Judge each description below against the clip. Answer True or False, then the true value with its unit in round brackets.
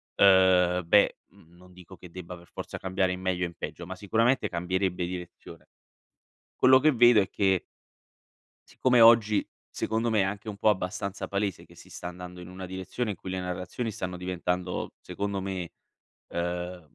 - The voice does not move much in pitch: True (2.2 semitones)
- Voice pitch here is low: True (95 Hz)